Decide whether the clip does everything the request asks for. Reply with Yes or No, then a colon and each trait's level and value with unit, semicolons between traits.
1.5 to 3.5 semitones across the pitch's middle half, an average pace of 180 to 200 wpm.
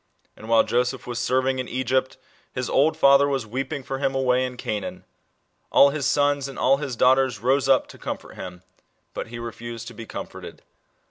Yes: narrow, 2.4 semitones; average, 195 wpm